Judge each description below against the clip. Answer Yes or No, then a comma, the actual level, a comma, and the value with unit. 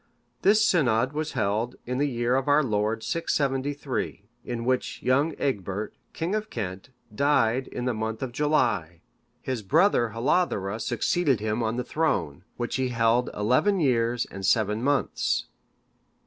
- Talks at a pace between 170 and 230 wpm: No, average, 150 wpm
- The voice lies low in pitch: Yes, low, 125 Hz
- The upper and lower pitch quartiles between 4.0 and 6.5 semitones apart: Yes, average, 4.6 semitones